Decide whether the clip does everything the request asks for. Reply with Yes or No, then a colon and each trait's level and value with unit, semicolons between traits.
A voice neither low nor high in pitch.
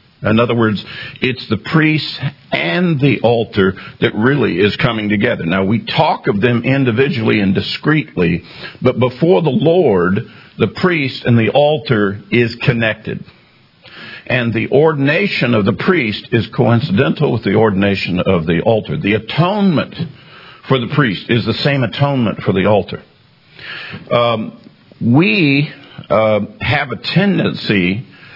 No: low, 120 Hz